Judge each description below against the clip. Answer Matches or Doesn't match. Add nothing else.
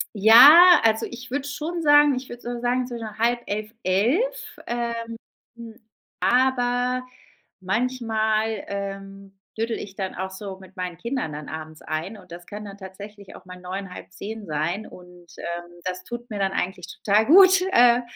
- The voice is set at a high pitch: Matches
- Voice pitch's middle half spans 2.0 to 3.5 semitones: Doesn't match